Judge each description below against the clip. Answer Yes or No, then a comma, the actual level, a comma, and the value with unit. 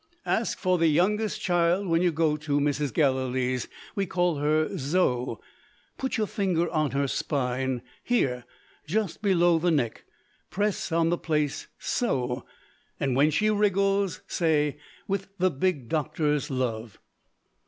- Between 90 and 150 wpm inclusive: Yes, average, 140 wpm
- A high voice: No, medium, 160 Hz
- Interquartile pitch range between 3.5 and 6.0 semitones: Yes, average, 5.1 semitones